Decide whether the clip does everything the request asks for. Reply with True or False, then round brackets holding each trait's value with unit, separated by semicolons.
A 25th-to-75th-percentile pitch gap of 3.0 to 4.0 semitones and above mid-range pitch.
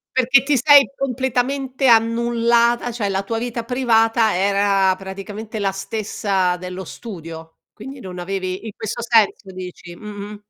True (3.7 semitones; 220 Hz)